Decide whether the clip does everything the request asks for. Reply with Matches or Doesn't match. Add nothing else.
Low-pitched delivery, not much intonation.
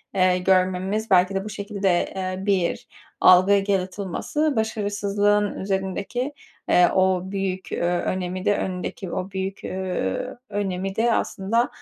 Doesn't match